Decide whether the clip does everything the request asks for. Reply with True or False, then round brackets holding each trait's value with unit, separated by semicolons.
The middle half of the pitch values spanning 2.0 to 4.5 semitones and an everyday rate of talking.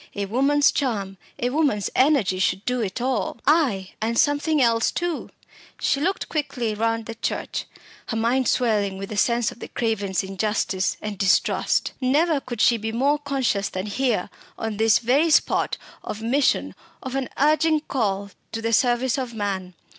False (4.9 semitones; 170 wpm)